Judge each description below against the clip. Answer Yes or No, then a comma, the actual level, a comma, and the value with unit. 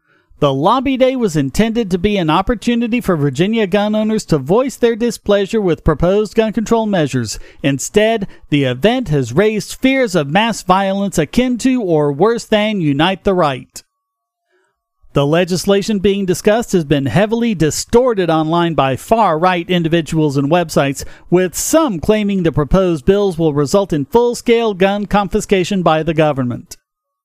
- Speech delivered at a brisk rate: No, average, 155 wpm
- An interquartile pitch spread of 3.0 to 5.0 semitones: No, wide, 5.6 semitones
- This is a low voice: No, high, 195 Hz